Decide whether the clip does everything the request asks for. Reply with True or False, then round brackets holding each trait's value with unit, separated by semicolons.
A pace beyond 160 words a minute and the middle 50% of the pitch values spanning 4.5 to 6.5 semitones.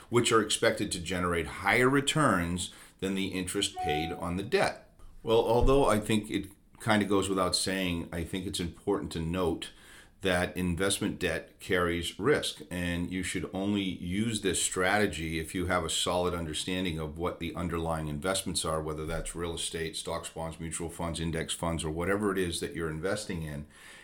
False (180 wpm; 2.8 semitones)